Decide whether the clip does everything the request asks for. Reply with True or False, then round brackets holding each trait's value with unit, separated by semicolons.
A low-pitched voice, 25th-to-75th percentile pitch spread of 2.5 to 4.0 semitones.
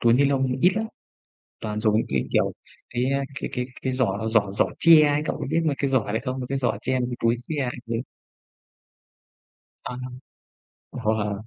True (125 Hz; 3.7 semitones)